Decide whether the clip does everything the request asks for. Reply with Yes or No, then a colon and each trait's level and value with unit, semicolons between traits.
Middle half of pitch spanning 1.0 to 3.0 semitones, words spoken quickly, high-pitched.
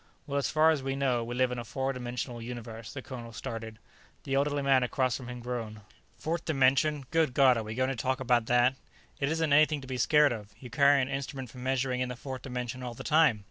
No: narrow, 2.4 semitones; fast, 240 wpm; low, 130 Hz